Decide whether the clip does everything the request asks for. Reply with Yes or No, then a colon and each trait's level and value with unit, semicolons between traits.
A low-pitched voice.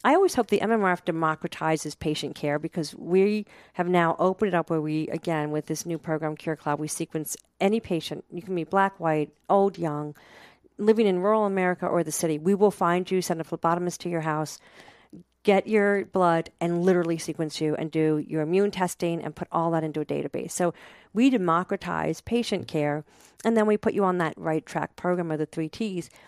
No: medium, 170 Hz